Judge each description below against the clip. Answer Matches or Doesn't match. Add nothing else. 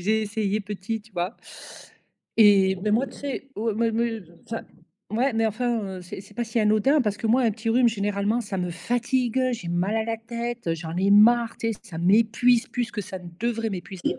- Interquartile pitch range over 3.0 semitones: Doesn't match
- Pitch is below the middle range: Doesn't match